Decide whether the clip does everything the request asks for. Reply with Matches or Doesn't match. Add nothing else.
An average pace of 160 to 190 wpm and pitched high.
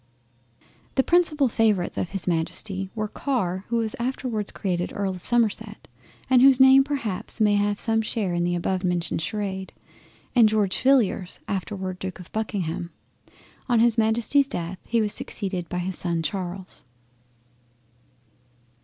Doesn't match